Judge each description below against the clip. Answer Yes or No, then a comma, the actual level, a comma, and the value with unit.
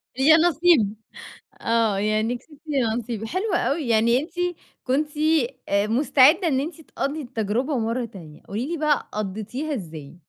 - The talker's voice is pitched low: No, high, 245 Hz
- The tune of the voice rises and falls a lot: Yes, wide, 5.7 semitones